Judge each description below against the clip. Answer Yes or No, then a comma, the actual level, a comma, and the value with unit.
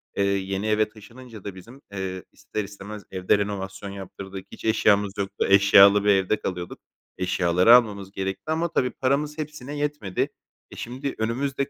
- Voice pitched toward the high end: No, low, 100 Hz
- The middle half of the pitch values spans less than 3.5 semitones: No, average, 4.2 semitones